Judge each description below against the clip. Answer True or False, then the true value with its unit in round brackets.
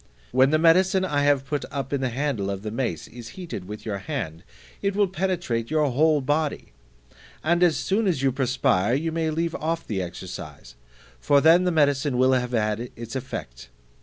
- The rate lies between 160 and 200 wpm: True (190 wpm)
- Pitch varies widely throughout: True (5.7 semitones)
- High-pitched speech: False (140 Hz)